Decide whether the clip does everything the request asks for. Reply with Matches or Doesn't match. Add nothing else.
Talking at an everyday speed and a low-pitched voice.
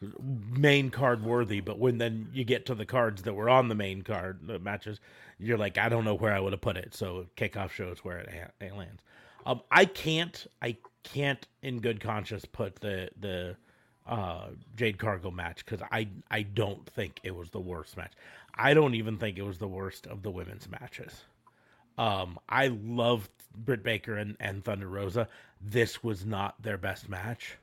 Matches